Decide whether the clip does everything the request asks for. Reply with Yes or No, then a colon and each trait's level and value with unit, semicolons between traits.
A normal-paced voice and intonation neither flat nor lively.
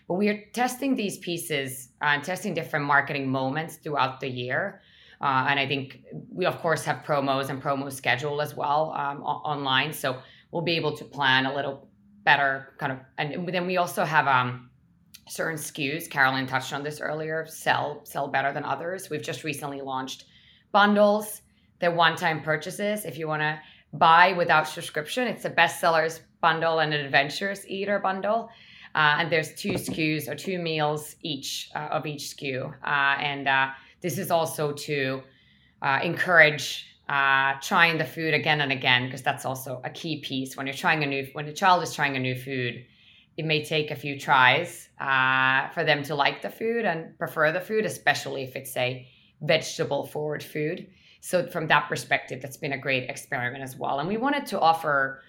Yes: average, 190 wpm; average, 3.5 semitones